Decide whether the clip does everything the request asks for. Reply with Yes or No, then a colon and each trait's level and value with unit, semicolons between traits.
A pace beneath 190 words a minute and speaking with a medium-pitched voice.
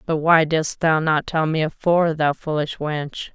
No: average, 195 wpm; medium, 155 Hz